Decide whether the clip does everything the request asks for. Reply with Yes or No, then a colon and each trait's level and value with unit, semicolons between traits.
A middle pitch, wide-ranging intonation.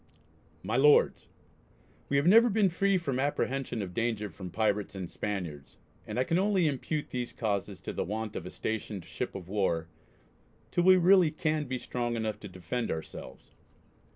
No: low, 120 Hz; wide, 7.3 semitones